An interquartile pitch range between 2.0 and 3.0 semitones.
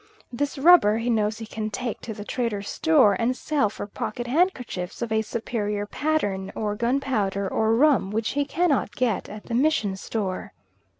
No: average, 4.4 semitones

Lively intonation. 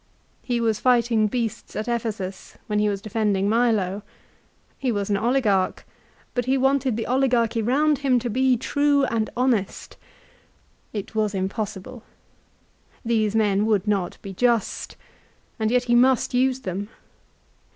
No: average, 3.2 semitones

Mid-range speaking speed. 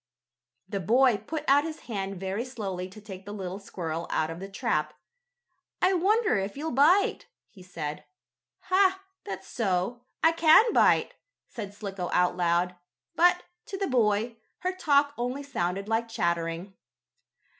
Yes: average, 150 wpm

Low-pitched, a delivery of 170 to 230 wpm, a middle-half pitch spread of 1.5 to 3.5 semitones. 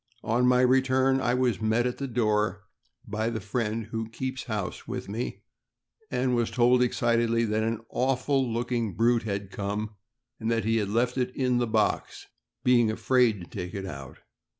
Yes: low, 115 Hz; average, 175 wpm; narrow, 2.6 semitones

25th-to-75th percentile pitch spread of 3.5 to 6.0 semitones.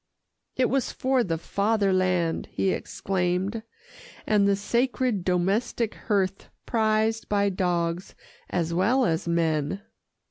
Yes: average, 3.9 semitones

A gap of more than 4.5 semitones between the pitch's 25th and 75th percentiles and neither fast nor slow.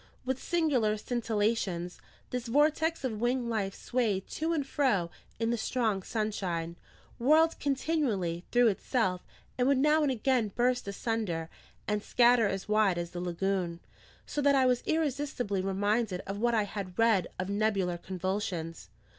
Yes: average, 4.9 semitones; average, 150 wpm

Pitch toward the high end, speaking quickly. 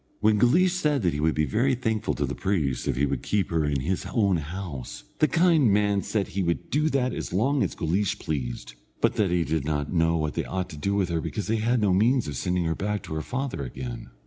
No: very low, 95 Hz; fast, 250 wpm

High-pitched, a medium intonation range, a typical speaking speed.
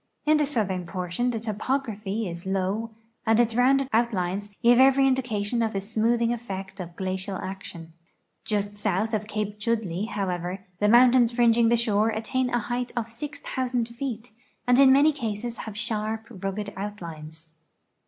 Yes: high, 220 Hz; average, 3.6 semitones; average, 155 wpm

